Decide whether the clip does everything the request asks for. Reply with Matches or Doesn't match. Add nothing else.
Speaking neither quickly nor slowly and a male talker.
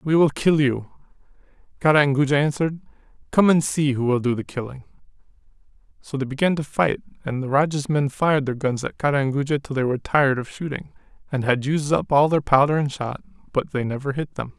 Doesn't match